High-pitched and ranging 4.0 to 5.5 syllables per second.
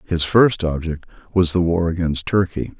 No: very low, 85 Hz; 4.8 syllables/s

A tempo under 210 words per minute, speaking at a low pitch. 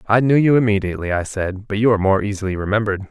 No: fast, 230 wpm; low, 105 Hz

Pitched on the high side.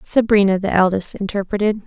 Yes: high, 200 Hz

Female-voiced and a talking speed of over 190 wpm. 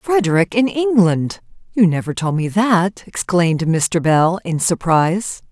No: female; average, 140 wpm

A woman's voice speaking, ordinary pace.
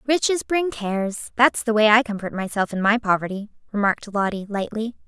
Yes: female; average, 175 wpm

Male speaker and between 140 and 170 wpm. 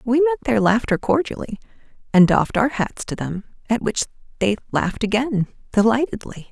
No: female; average, 155 wpm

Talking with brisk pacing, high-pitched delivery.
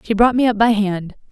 Yes: fast, 275 wpm; high, 215 Hz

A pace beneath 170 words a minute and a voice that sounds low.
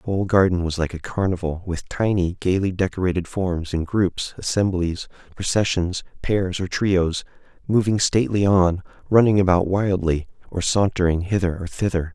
Yes: average, 150 wpm; very low, 90 Hz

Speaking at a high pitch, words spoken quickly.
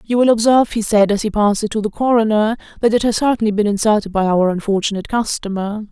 Yes: high, 215 Hz; fast, 225 wpm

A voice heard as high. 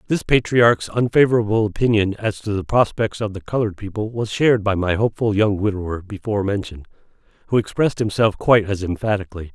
No: low, 105 Hz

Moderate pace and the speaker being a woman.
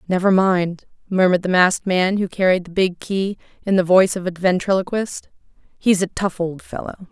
Yes: average, 185 wpm; female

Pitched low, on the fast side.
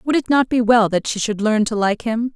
No: high, 230 Hz; fast, 305 wpm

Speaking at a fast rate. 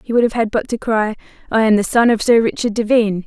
Yes: fast, 275 wpm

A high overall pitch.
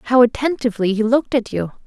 Yes: high, 240 Hz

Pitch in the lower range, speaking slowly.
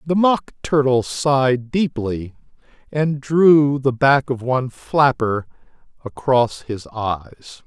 Yes: low, 130 Hz; slow, 115 wpm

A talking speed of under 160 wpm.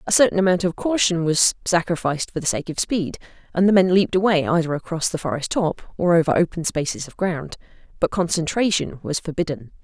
No: average, 195 wpm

